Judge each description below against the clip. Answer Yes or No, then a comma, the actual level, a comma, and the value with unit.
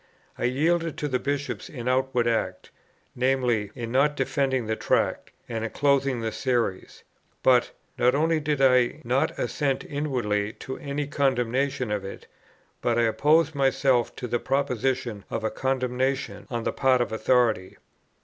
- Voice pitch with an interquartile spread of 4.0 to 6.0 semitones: No, average, 2.8 semitones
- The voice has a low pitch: Yes, low, 130 Hz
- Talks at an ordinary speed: Yes, average, 155 wpm